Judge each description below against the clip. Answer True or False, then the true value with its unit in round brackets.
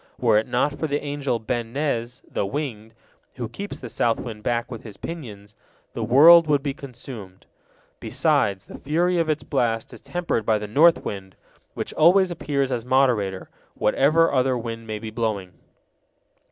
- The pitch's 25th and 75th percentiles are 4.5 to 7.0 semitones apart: True (4.9 semitones)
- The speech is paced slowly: False (170 wpm)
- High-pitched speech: False (125 Hz)